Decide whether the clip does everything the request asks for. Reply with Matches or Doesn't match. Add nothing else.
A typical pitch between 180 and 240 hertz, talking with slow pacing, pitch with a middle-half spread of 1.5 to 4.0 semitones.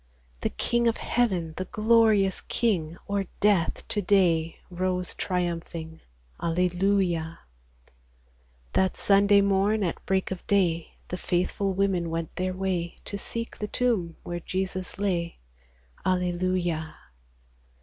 Matches